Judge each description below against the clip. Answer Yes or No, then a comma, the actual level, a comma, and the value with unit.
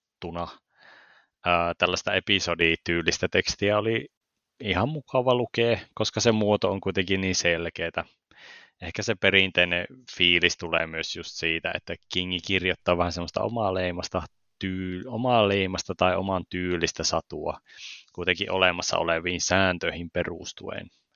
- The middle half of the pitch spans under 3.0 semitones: Yes, narrow, 2.6 semitones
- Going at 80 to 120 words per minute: Yes, average, 110 wpm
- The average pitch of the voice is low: Yes, very low, 90 Hz